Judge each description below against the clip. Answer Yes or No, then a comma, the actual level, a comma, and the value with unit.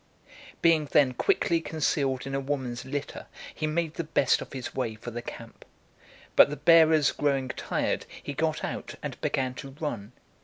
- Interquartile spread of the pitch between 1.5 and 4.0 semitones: Yes, average, 3.2 semitones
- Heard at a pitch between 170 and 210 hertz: No, medium, 140 Hz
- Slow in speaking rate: No, average, 175 wpm